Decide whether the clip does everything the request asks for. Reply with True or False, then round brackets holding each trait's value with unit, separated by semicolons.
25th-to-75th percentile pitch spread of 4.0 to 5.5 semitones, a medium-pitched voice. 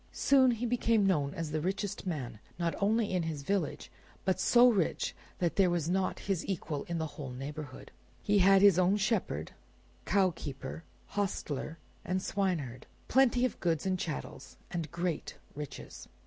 True (4.7 semitones; 180 Hz)